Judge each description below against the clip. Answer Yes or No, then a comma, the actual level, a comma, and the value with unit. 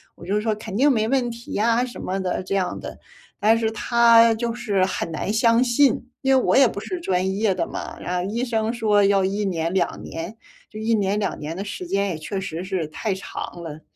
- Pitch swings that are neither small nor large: Yes, average, 3.7 semitones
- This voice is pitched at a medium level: No, high, 210 Hz